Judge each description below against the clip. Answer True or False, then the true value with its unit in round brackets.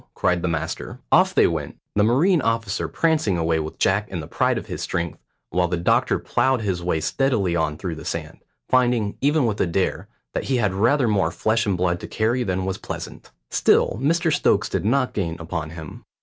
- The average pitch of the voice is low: True (100 Hz)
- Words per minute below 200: False (205 wpm)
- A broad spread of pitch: True (5.9 semitones)